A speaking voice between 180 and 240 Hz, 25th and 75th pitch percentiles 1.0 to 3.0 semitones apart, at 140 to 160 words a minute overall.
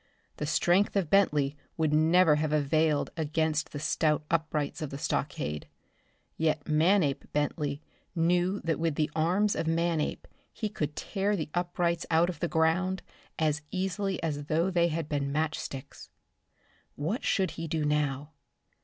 No: medium, 160 Hz; average, 2.7 semitones; average, 155 wpm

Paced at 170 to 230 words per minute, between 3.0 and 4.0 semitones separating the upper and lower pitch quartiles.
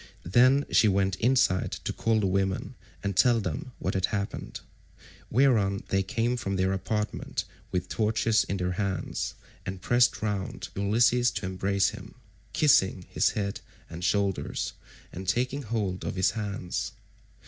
No: average, 150 wpm; average, 3.3 semitones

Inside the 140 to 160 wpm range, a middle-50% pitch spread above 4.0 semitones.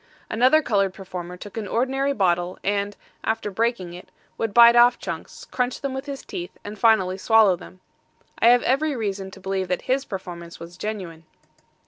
No: average, 175 wpm; average, 4.5 semitones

